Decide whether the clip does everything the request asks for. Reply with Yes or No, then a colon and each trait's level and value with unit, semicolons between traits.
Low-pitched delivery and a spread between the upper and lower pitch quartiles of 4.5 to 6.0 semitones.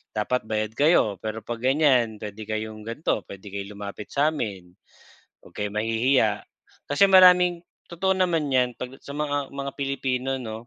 Yes: low, 125 Hz; average, 5.1 semitones